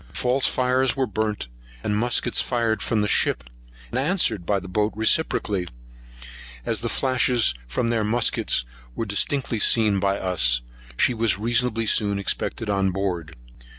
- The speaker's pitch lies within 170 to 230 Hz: No, low, 110 Hz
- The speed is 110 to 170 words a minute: Yes, average, 150 wpm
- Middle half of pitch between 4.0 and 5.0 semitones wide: No, average, 3.6 semitones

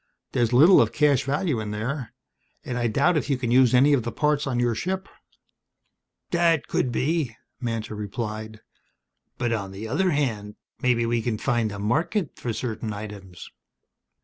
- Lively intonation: No, average, 4.7 semitones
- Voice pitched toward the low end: Yes, low, 120 Hz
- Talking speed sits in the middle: Yes, average, 170 wpm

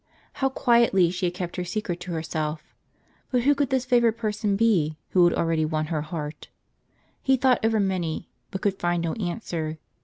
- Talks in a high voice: No, medium, 180 Hz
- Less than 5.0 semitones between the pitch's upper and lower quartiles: No, wide, 5.6 semitones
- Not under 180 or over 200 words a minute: Yes, average, 185 wpm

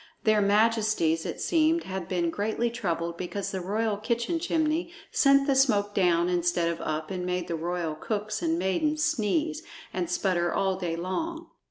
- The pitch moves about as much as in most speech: No, wide, 7.5 semitones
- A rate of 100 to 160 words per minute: No, average, 170 wpm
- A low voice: No, high, 200 Hz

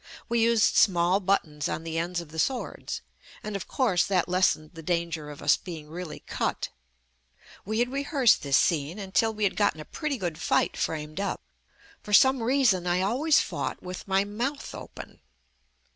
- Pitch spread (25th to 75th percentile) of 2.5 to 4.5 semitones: No, average, 5.3 semitones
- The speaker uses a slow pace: No, average, 175 wpm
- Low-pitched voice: No, high, 190 Hz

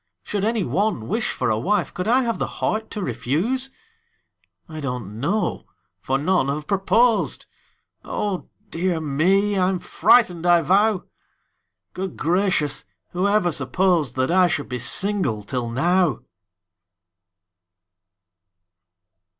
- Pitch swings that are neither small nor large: No, wide, 6.1 semitones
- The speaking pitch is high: No, medium, 180 Hz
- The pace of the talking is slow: Yes, slow, 125 wpm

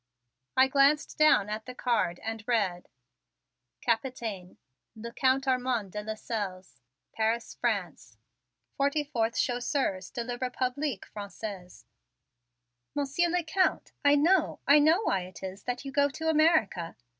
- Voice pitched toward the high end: Yes, high, 245 Hz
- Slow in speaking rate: Yes, slow, 130 wpm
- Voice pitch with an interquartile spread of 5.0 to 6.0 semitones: Yes, average, 5.3 semitones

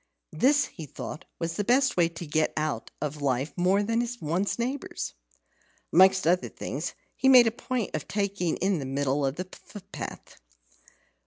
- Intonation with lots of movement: Yes, wide, 6.7 semitones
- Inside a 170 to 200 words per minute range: No, average, 155 wpm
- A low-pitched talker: No, medium, 185 Hz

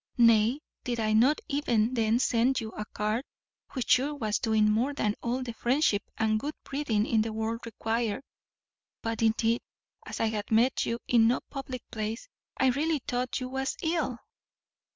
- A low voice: No, high, 235 Hz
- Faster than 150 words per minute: Yes, average, 170 wpm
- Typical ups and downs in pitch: Yes, average, 3.0 semitones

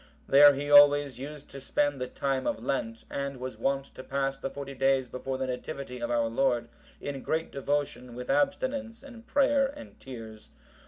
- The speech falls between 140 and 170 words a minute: No, average, 180 wpm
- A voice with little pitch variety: Yes, narrow, 2.3 semitones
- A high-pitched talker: No, low, 135 Hz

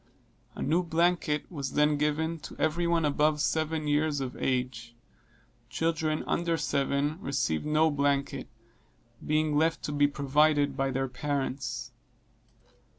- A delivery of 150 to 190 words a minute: No, slow, 135 wpm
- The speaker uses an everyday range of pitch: No, narrow, 2.1 semitones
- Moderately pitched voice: Yes, medium, 150 Hz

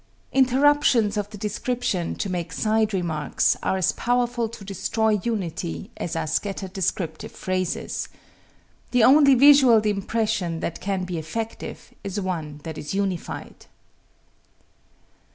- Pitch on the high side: Yes, high, 200 Hz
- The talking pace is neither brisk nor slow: No, slow, 125 wpm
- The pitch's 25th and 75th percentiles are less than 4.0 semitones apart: No, average, 4.6 semitones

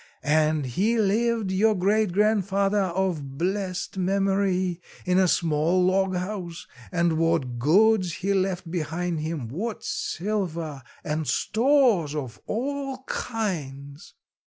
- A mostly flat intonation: No, average, 4.3 semitones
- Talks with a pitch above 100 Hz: Yes, medium, 185 Hz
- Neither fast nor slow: No, slow, 115 wpm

